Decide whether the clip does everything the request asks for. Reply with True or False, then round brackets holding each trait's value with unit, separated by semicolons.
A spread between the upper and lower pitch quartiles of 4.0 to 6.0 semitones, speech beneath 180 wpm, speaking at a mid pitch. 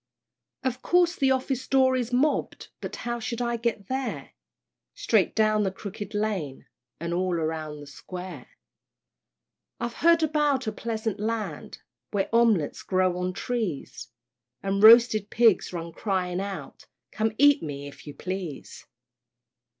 False (5.1 semitones; 140 wpm; 215 Hz)